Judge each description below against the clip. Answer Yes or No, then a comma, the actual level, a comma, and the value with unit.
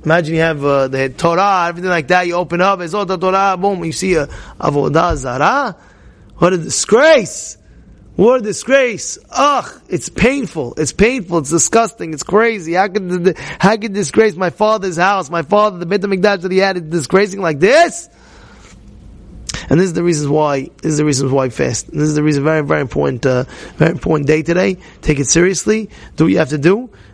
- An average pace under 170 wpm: No, average, 200 wpm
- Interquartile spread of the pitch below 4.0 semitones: No, average, 4.3 semitones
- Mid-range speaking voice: Yes, medium, 175 Hz